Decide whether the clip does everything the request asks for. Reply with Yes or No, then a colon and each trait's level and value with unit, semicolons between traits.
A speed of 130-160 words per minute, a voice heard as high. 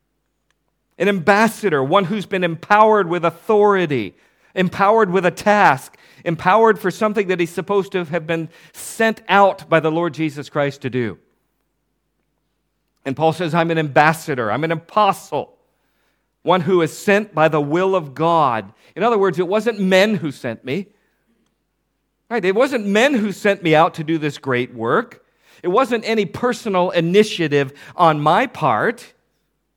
No: average, 155 wpm; medium, 180 Hz